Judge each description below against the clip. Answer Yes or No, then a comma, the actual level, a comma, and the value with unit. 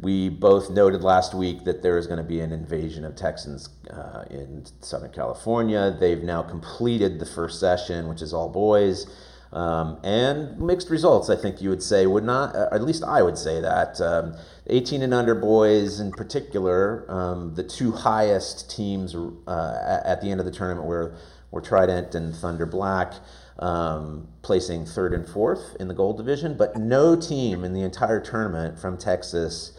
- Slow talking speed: No, average, 180 wpm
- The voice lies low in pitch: Yes, very low, 90 Hz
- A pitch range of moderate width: Yes, average, 3.6 semitones